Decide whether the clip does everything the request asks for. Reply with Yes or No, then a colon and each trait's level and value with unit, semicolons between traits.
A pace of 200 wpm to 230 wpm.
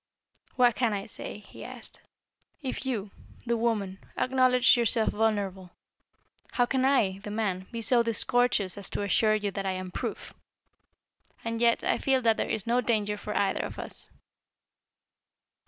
No: average, 160 wpm